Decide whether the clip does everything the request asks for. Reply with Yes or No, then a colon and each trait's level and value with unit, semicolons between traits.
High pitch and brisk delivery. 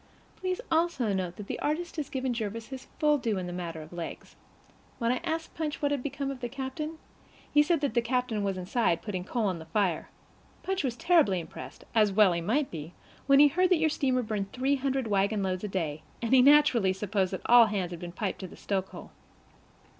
Yes: high, 230 Hz; fast, 220 wpm